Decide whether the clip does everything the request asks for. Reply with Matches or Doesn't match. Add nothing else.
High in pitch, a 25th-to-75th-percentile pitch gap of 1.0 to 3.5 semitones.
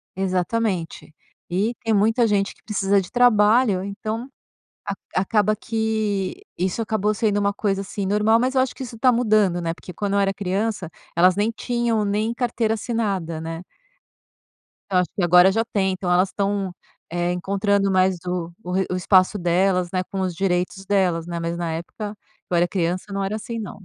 Matches